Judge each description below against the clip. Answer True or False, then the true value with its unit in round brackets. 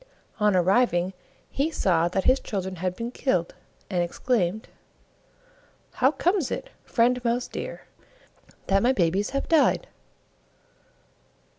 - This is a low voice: False (210 Hz)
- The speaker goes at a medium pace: False (120 wpm)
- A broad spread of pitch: True (5.7 semitones)